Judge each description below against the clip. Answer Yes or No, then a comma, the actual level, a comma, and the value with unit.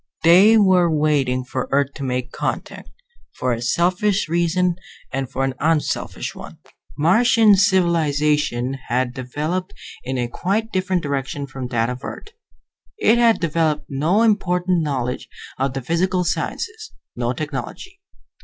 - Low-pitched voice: No, medium, 155 Hz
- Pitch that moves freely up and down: Yes, wide, 5.7 semitones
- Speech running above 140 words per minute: No, slow, 135 wpm